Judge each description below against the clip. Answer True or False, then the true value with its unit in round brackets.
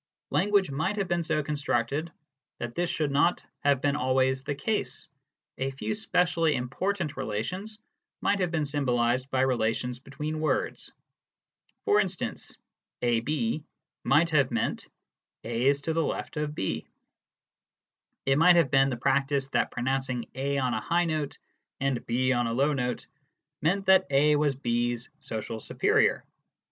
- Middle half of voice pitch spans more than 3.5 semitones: True (4.1 semitones)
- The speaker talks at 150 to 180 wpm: True (155 wpm)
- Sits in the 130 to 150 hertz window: True (140 Hz)